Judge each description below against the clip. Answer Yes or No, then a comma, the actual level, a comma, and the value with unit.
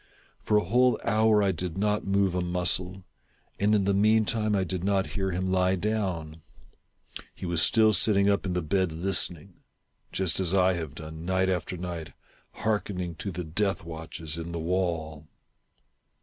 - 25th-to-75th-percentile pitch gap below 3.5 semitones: Yes, average, 2.8 semitones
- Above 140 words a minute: Yes, average, 180 wpm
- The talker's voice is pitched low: Yes, very low, 95 Hz